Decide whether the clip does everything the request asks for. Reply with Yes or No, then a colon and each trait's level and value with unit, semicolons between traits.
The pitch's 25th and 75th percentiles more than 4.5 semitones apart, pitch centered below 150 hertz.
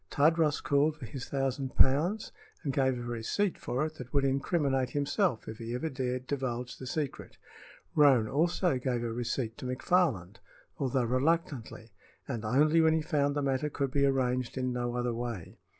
No: average, 3.3 semitones; low, 135 Hz